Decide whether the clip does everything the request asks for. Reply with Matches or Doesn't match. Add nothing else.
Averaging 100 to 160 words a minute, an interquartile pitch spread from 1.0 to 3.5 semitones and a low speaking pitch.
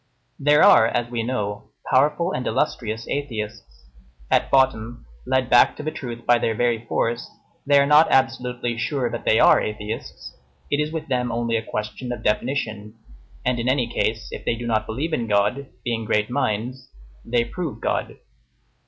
Doesn't match